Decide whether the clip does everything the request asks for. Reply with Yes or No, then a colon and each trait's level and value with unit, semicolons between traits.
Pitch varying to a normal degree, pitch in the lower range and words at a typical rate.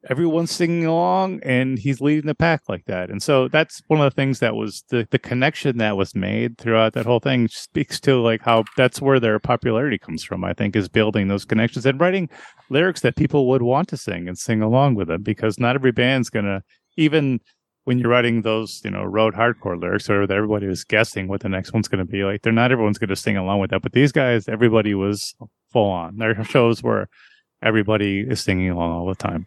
No: average, 4.9 semitones; low, 115 Hz; fast, 230 wpm